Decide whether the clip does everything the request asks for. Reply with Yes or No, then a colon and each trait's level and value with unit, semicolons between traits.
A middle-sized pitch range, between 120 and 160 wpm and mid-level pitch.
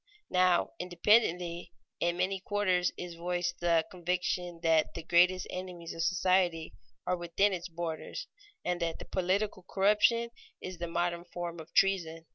No: narrow, 1.5 semitones; average, 140 wpm; medium, 175 Hz